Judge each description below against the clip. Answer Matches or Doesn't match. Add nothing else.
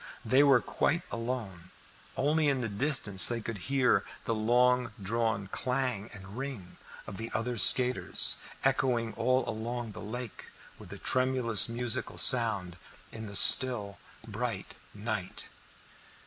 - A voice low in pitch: Matches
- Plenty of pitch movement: Doesn't match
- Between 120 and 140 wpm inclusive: Matches